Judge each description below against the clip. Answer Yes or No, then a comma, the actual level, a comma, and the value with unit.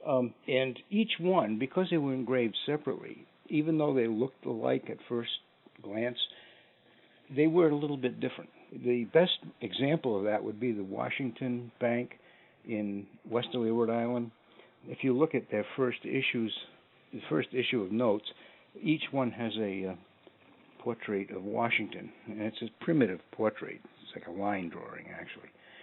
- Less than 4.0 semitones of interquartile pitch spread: Yes, average, 3.5 semitones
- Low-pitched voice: Yes, low, 120 Hz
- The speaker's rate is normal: Yes, average, 160 wpm